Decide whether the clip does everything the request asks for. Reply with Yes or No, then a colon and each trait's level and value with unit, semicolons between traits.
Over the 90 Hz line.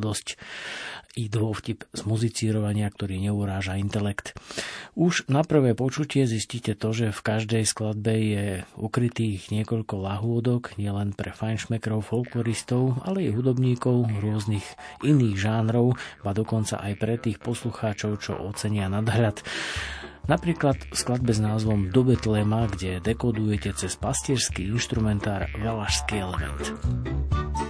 Yes: low, 110 Hz